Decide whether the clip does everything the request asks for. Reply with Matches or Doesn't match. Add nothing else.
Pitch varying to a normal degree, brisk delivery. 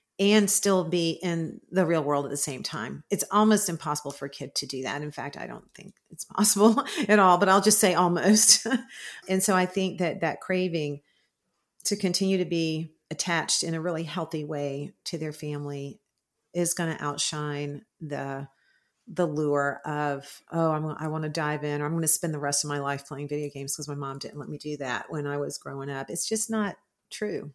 Matches